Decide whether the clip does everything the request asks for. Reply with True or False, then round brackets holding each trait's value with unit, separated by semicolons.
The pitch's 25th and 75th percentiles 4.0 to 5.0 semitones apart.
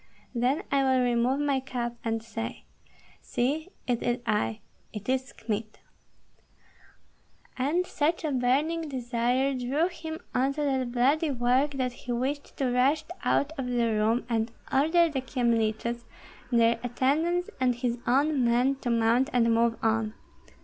False (3.0 semitones)